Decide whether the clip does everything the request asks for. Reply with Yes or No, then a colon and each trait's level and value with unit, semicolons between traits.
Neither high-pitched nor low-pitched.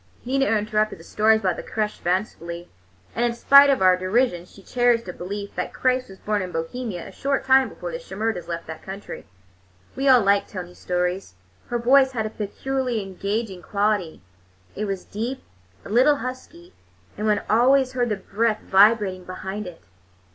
No: high, 215 Hz